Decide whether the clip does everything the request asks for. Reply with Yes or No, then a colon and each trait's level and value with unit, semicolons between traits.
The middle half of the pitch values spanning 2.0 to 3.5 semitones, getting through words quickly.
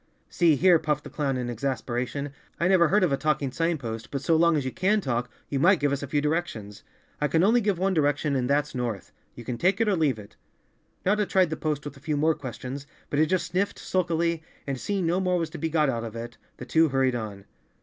No: average, 4.7 semitones; fast, 245 wpm